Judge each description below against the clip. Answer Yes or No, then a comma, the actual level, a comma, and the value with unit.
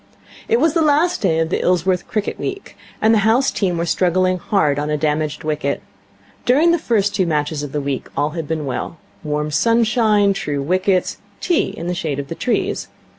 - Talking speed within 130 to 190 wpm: No, average, 200 wpm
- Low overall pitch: No, medium, 180 Hz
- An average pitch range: No, wide, 6.5 semitones